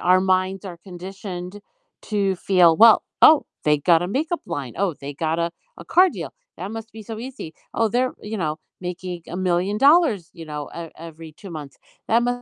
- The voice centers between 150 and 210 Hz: Yes, medium, 185 Hz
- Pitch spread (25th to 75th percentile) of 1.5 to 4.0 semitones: No, average, 4.5 semitones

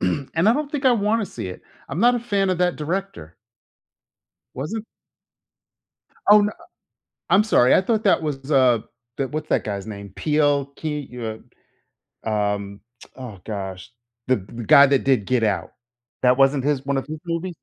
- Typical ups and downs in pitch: No, wide, 8.8 semitones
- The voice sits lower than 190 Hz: Yes, medium, 140 Hz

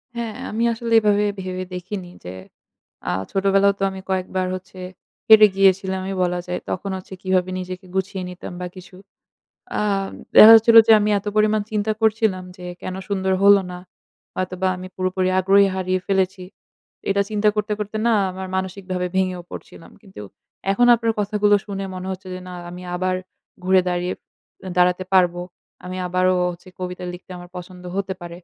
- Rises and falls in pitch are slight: Yes, narrow, 1.7 semitones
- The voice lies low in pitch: No, high, 190 Hz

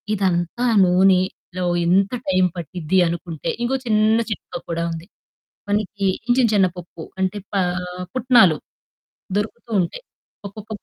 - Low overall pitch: No, high, 190 Hz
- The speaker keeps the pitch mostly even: No, average, 3.4 semitones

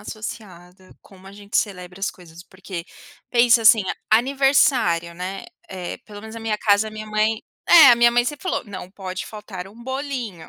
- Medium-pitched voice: No, high, 210 Hz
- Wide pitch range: No, average, 4.1 semitones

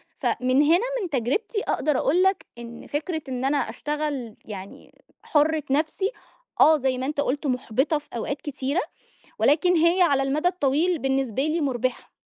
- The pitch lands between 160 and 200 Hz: No, very high, 290 Hz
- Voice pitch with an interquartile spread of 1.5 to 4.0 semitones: Yes, average, 3.4 semitones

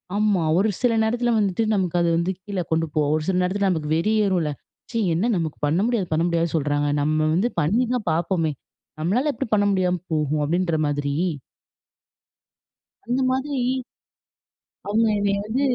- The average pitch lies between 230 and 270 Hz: No, medium, 185 Hz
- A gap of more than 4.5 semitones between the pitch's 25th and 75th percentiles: Yes, average, 5.2 semitones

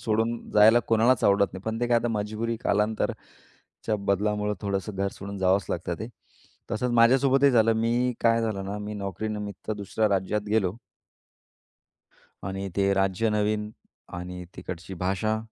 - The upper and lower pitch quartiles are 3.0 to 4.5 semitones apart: No, narrow, 2.4 semitones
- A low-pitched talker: Yes, low, 105 Hz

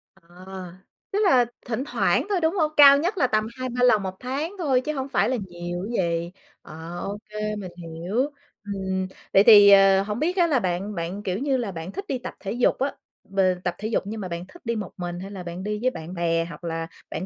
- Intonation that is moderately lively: No, wide, 6.4 semitones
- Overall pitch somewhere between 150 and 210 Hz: Yes, high, 205 Hz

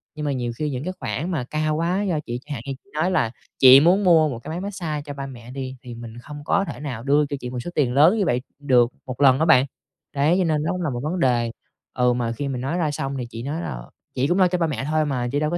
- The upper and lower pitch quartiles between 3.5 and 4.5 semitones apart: Yes, average, 4.2 semitones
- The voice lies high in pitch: No, medium, 145 Hz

